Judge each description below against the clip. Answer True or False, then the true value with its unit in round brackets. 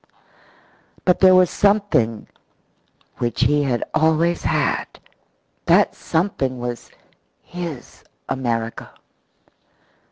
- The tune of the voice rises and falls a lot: True (6.6 semitones)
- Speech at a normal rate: False (85 wpm)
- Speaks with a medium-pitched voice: True (145 Hz)